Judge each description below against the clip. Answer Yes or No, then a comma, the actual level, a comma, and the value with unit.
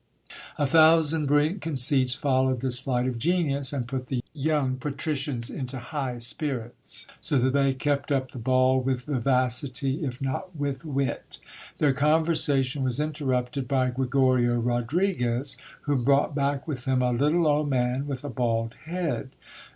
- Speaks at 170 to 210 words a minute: No, average, 155 wpm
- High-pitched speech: No, low, 135 Hz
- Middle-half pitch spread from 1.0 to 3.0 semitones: Yes, narrow, 2.5 semitones